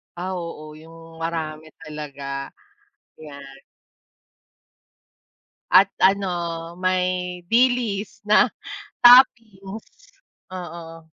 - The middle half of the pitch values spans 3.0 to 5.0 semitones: Yes, average, 3.5 semitones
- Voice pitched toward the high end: No, medium, 175 Hz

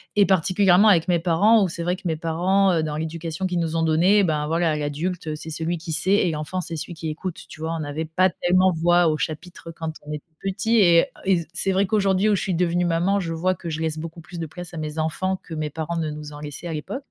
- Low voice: No, medium, 170 Hz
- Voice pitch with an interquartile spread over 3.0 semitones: No, average, 2.7 semitones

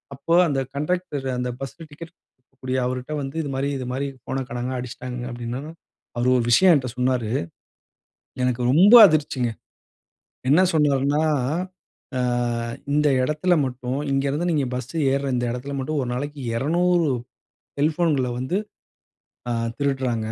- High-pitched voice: No, low, 135 Hz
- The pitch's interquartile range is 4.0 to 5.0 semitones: No, average, 3.2 semitones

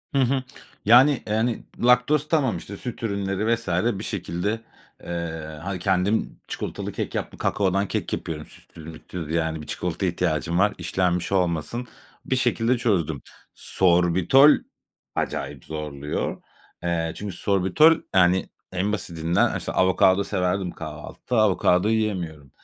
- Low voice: Yes, very low, 95 Hz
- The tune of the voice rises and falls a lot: No, average, 4.6 semitones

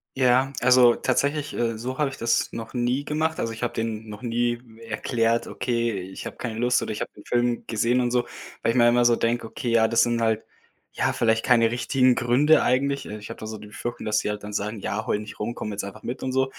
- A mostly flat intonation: Yes, narrow, 2.0 semitones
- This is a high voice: No, low, 120 Hz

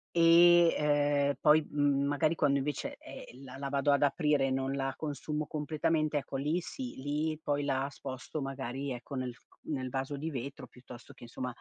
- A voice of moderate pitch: Yes, medium, 145 Hz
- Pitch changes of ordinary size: No, narrow, 2.1 semitones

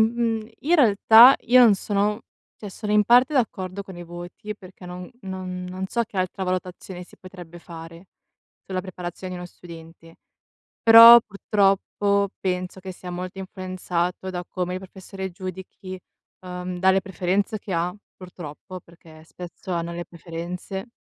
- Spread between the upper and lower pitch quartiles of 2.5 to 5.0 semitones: No, narrow, 2.1 semitones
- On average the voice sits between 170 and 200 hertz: Yes, medium, 185 Hz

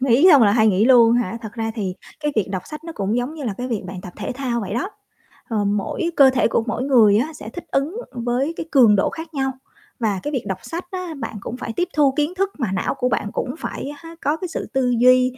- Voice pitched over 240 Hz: Yes, very high, 250 Hz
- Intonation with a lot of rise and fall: No, average, 5.0 semitones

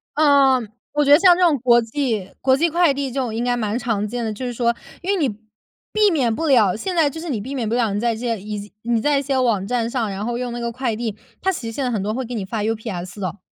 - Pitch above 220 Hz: Yes, high, 240 Hz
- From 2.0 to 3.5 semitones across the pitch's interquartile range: No, average, 4.1 semitones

